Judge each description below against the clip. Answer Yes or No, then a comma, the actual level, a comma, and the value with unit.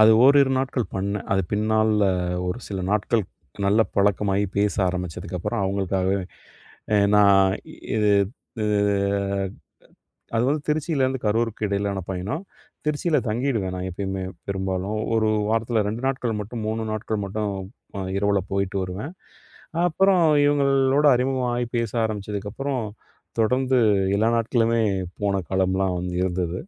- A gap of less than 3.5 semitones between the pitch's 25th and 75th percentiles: No, average, 4.0 semitones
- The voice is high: No, low, 105 Hz